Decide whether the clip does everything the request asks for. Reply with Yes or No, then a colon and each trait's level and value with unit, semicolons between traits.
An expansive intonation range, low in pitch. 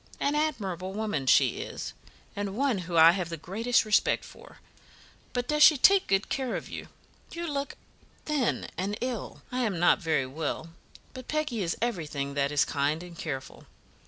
No: wide, 7.8 semitones; high, 195 Hz